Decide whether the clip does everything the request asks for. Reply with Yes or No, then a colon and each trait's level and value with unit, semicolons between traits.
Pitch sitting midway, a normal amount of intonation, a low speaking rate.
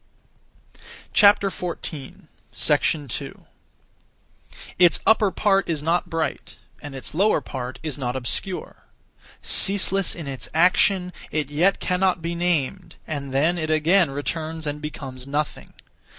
Yes: medium, 160 Hz; average, 3.9 semitones; slow, 115 wpm